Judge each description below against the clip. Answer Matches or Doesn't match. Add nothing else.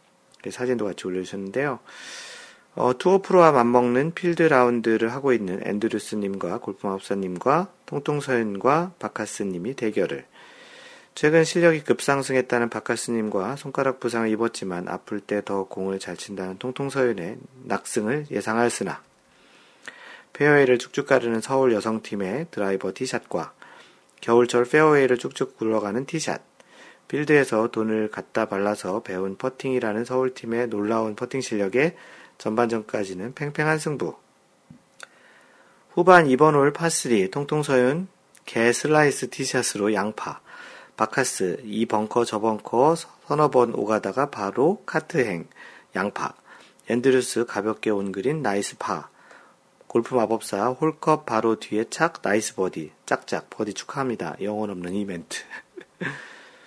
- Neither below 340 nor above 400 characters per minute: Doesn't match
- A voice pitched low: Matches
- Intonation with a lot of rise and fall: Doesn't match